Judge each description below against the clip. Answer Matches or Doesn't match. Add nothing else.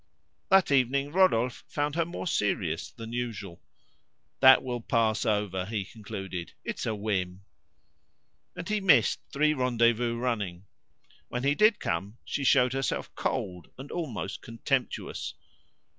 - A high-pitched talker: Doesn't match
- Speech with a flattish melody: Doesn't match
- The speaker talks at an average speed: Doesn't match